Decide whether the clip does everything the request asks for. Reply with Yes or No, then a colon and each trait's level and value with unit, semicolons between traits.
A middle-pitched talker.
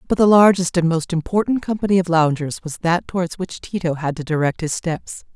Yes: medium, 170 Hz